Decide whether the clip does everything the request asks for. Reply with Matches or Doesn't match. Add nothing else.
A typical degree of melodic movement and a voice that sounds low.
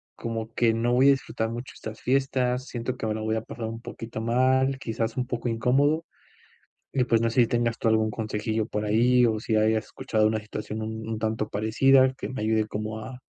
Doesn't match